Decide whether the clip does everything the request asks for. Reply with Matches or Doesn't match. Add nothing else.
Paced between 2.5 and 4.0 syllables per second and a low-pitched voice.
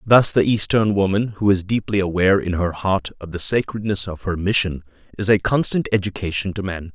Doesn't match